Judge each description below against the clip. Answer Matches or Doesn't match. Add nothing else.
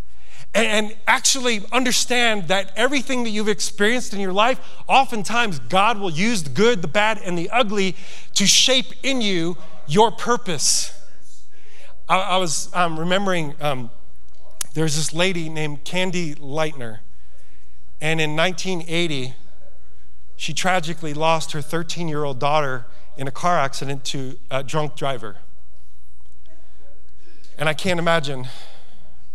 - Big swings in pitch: Matches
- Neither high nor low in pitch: Matches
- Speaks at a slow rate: Matches